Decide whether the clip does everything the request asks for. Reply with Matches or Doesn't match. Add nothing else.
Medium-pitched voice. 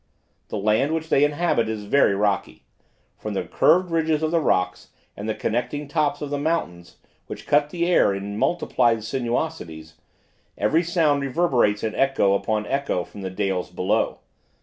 Doesn't match